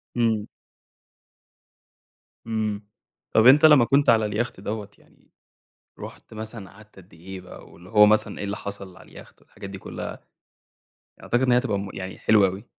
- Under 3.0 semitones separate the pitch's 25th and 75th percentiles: Yes, narrow, 2.6 semitones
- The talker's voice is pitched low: Yes, low, 105 Hz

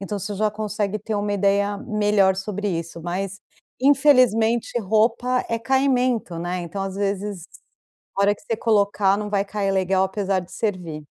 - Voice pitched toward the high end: Yes, high, 205 Hz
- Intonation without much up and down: Yes, narrow, 2.1 semitones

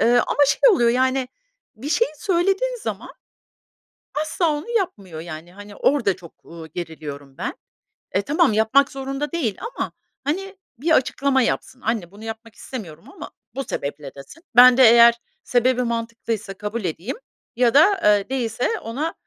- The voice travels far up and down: Yes, wide, 5.7 semitones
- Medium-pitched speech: No, high, 235 Hz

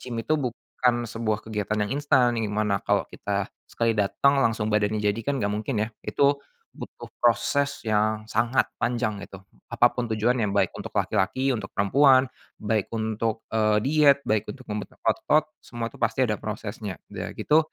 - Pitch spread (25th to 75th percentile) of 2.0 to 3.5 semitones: Yes, average, 3.1 semitones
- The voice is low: Yes, low, 110 Hz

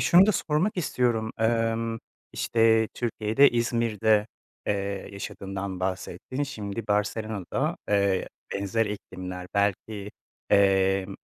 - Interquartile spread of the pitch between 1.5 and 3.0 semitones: Yes, average, 2.7 semitones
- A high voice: No, low, 105 Hz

